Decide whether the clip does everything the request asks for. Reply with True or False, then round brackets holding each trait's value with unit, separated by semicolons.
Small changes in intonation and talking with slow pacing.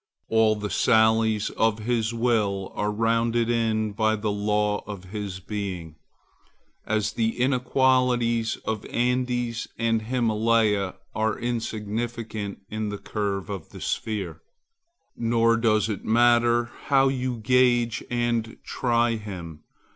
True (2.1 semitones; 120 wpm)